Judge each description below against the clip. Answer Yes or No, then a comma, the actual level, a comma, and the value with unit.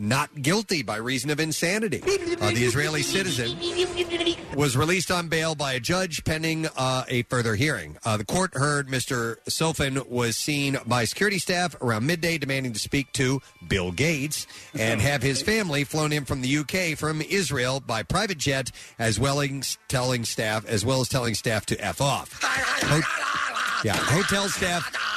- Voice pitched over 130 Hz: Yes, medium, 140 Hz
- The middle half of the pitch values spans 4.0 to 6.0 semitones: Yes, average, 4.9 semitones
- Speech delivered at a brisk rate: No, average, 170 wpm